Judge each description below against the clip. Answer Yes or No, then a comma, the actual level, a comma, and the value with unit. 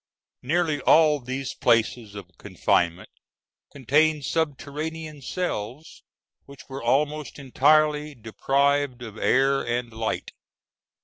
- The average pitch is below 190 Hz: Yes, medium, 140 Hz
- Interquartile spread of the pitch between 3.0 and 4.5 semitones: Yes, average, 3.9 semitones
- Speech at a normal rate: No, slow, 100 wpm